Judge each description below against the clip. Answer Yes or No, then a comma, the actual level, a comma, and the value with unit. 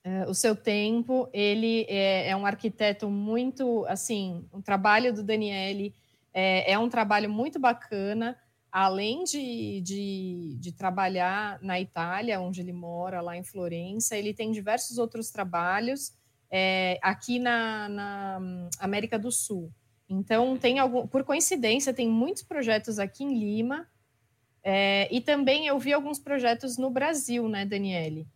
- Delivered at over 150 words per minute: No, average, 140 wpm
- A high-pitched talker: Yes, high, 210 Hz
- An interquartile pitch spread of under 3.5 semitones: No, average, 4.1 semitones